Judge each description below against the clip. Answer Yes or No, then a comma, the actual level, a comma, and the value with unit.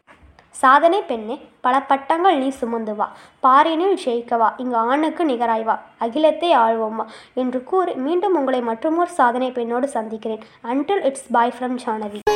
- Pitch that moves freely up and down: No, average, 4.8 semitones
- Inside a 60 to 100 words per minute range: No, fast, 130 wpm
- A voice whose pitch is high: Yes, very high, 255 Hz